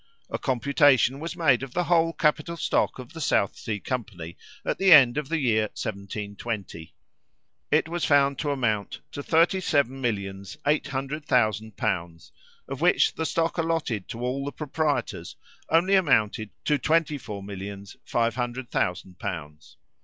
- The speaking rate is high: No, average, 160 wpm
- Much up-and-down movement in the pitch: Yes, wide, 6.6 semitones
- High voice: No, low, 130 Hz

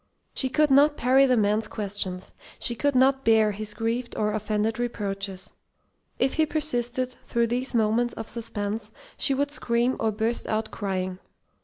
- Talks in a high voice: Yes, high, 230 Hz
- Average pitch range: Yes, average, 3.3 semitones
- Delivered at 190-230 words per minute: No, average, 160 wpm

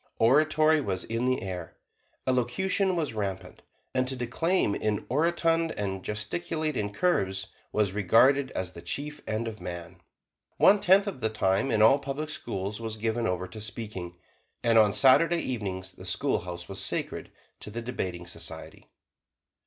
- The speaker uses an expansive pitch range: Yes, wide, 7.1 semitones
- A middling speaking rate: Yes, average, 155 wpm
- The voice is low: Yes, low, 110 Hz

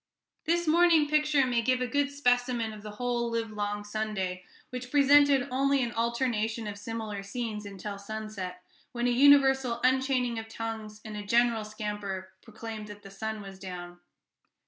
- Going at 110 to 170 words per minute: Yes, average, 160 wpm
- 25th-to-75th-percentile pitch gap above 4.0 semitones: No, average, 3.4 semitones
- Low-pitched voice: No, high, 225 Hz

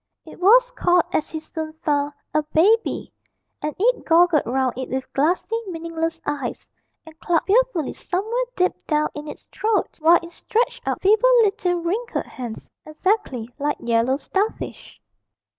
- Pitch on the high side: Yes, very high, 335 Hz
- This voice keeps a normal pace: Yes, average, 150 wpm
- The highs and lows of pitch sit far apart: Yes, wide, 5.7 semitones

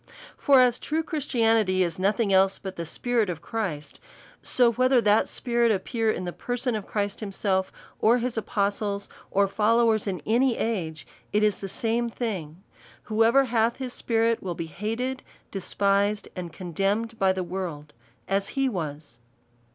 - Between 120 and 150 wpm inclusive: No, average, 165 wpm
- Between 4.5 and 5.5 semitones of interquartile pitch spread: No, average, 3.7 semitones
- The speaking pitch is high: Yes, high, 210 Hz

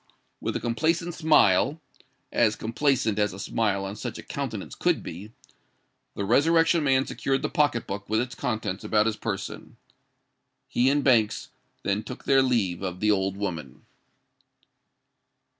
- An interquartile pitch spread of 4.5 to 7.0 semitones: Yes, average, 5.2 semitones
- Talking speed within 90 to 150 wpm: Yes, average, 140 wpm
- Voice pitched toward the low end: Yes, low, 110 Hz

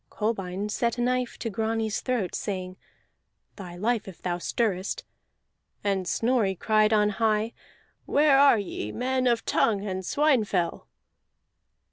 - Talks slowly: Yes, slow, 130 wpm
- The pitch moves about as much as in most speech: Yes, average, 3.8 semitones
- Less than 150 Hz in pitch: No, high, 215 Hz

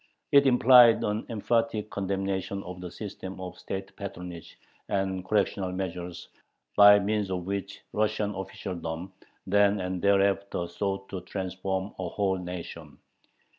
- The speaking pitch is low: Yes, very low, 95 Hz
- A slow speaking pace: Yes, slow, 130 wpm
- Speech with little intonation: Yes, narrow, 1.9 semitones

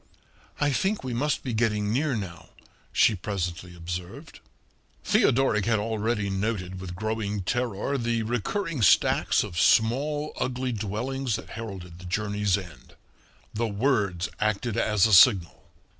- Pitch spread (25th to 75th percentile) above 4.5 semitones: No, average, 4.1 semitones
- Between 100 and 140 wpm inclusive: Yes, slow, 135 wpm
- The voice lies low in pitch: Yes, low, 110 Hz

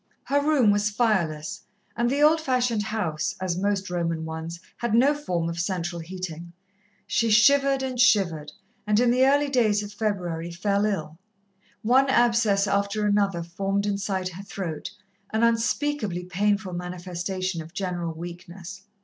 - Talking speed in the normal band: Yes, average, 150 wpm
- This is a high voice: Yes, high, 200 Hz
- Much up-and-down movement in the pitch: No, average, 4.8 semitones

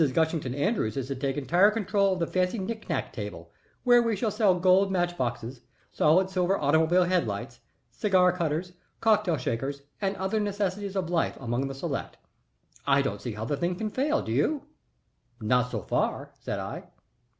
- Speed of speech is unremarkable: Yes, average, 180 wpm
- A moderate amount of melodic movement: No, wide, 6.4 semitones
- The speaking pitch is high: No, medium, 175 Hz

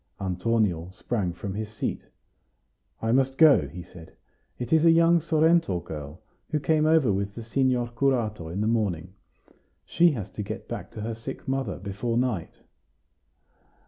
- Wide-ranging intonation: Yes, wide, 6.0 semitones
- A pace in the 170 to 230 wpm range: No, average, 160 wpm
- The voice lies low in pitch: Yes, low, 115 Hz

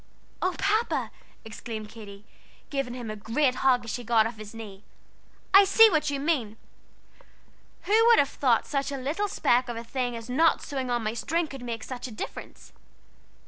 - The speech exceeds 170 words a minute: Yes, average, 185 wpm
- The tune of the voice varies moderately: Yes, average, 4.8 semitones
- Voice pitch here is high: Yes, very high, 250 Hz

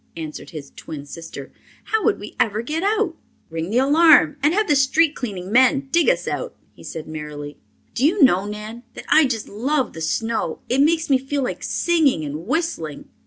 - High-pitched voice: Yes, very high, 255 Hz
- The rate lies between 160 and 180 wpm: No, average, 195 wpm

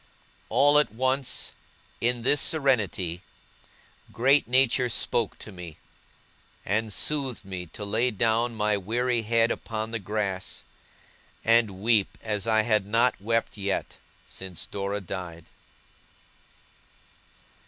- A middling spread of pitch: Yes, average, 3.4 semitones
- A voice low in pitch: Yes, low, 110 Hz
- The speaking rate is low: Yes, slow, 115 wpm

